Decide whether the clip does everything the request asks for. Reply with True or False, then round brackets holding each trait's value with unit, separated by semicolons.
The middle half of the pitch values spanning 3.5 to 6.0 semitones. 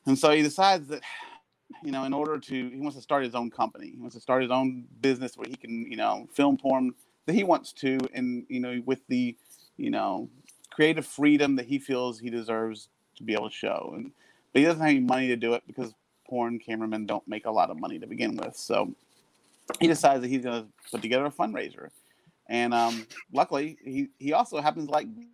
True (3.8 semitones)